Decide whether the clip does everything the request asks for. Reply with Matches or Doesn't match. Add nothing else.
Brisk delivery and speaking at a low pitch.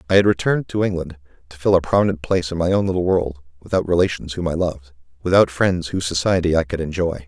Matches